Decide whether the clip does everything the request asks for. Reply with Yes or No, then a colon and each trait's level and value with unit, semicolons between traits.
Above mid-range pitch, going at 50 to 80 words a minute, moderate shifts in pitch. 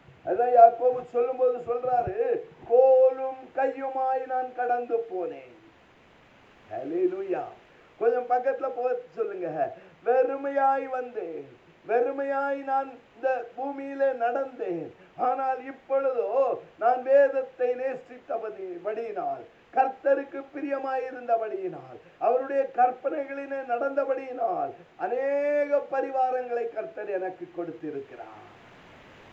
No: very high, 260 Hz; slow, 75 wpm; narrow, 2.0 semitones